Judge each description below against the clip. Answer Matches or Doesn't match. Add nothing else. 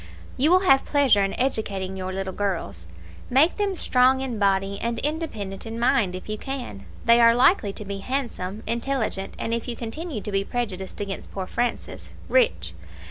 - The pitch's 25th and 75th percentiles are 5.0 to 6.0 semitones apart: Matches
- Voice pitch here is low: Doesn't match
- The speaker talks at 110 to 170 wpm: Doesn't match